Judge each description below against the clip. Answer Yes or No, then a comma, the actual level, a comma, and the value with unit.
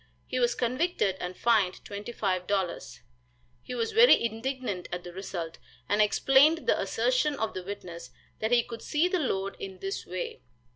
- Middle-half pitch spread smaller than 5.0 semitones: No, wide, 5.6 semitones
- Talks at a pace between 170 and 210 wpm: No, average, 160 wpm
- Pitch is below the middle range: No, high, 215 Hz